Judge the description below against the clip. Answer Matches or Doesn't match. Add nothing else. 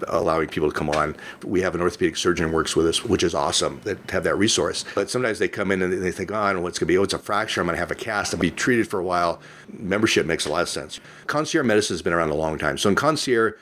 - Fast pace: Matches